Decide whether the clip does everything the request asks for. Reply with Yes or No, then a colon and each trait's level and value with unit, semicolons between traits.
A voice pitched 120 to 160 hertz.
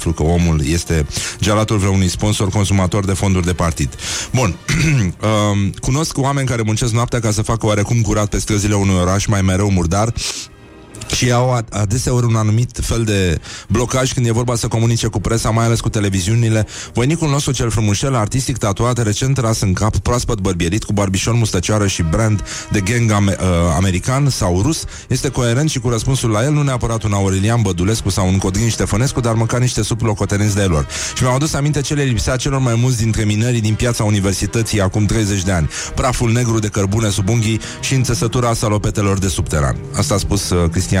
No: low, 110 Hz